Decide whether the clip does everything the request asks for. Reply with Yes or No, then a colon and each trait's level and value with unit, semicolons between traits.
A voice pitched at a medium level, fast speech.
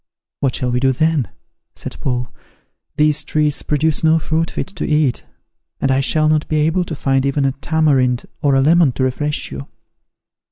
No: medium, 145 Hz; average, 190 wpm